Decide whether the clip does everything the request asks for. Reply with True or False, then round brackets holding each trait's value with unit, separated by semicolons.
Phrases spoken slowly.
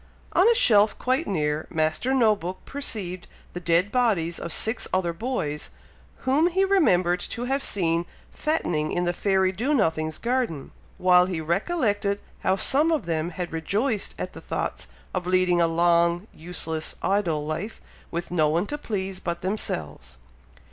False (160 wpm)